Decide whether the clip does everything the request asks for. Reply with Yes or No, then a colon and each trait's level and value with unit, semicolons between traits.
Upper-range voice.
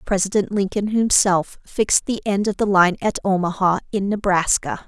Yes: high, 195 Hz